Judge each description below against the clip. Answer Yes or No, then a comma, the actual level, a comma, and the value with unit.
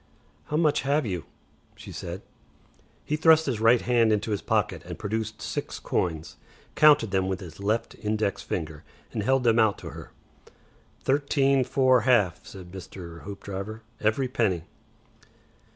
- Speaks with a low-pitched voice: Yes, low, 110 Hz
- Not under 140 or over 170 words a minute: Yes, average, 150 wpm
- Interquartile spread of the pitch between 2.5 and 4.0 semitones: No, wide, 5.4 semitones